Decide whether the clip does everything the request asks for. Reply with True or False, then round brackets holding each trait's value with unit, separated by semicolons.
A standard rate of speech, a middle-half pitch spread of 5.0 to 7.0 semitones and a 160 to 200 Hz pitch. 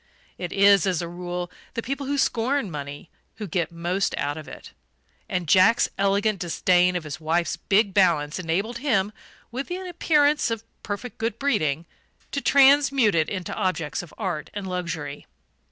True (165 wpm; 5.4 semitones; 190 Hz)